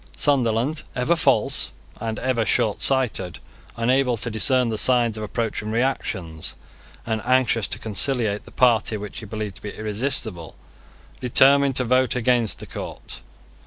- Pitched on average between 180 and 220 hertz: No, low, 115 Hz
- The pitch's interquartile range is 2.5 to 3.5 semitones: Yes, average, 3.0 semitones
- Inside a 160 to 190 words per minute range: No, average, 140 wpm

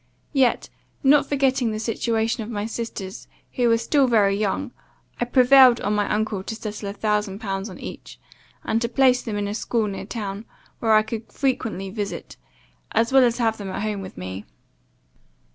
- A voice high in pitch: Yes, high, 220 Hz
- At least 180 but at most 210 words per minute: Yes, average, 185 wpm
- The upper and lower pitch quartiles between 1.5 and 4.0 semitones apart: Yes, average, 2.8 semitones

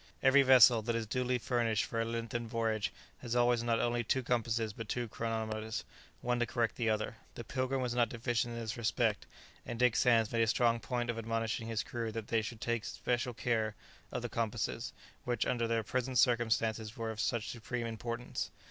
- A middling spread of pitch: No, narrow, 1.4 semitones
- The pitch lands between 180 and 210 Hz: No, low, 115 Hz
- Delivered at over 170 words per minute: Yes, average, 200 wpm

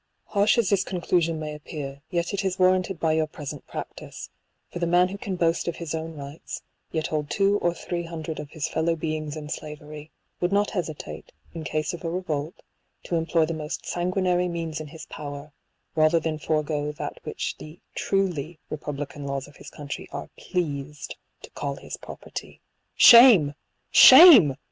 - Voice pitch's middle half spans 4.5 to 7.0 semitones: No, average, 3.0 semitones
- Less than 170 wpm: No, average, 175 wpm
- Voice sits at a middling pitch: Yes, medium, 160 Hz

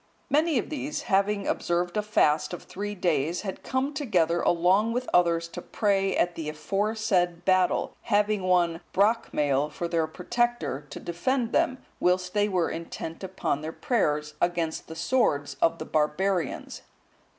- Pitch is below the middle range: No, medium, 180 Hz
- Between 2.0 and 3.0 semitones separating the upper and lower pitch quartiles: No, average, 4.1 semitones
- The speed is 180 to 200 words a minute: No, average, 150 wpm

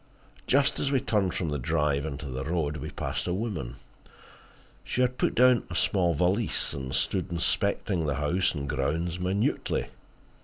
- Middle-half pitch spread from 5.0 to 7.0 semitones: Yes, average, 5.3 semitones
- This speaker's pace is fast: No, average, 165 wpm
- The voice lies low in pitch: Yes, very low, 85 Hz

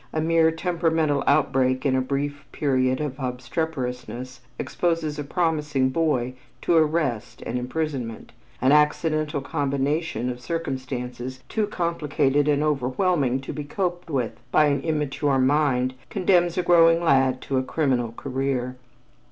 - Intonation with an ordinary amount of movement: Yes, average, 3.8 semitones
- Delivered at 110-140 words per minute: Yes, slow, 135 wpm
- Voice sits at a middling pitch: Yes, medium, 145 Hz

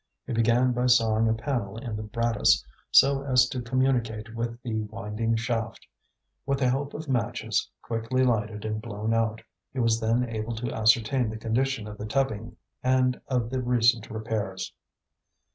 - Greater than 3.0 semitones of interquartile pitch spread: No, narrow, 2.4 semitones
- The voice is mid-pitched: No, low, 115 Hz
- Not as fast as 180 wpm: Yes, average, 165 wpm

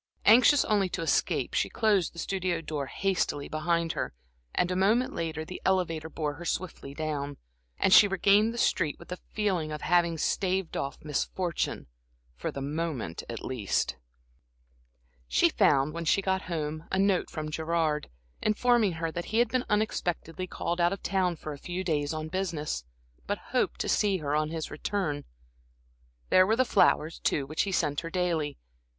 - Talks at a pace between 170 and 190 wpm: Yes, average, 175 wpm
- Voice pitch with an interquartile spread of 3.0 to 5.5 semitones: Yes, average, 3.8 semitones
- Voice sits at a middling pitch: Yes, medium, 170 Hz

